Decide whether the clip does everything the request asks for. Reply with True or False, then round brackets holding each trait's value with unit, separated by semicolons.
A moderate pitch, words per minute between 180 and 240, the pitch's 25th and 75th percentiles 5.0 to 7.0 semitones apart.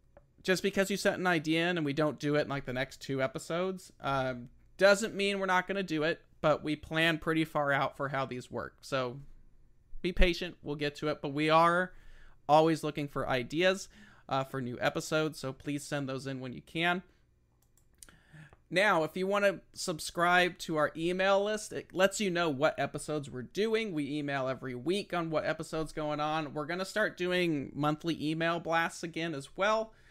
False (155 Hz; 200 wpm; 4.1 semitones)